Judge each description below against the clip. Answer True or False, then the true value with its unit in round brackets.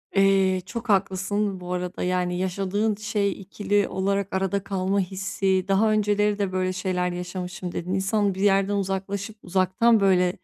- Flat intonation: True (1.5 semitones)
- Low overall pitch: False (195 Hz)